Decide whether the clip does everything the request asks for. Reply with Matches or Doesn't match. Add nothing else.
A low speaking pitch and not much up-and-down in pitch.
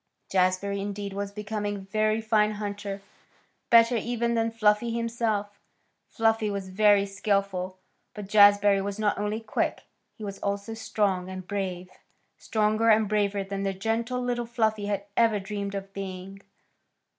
Doesn't match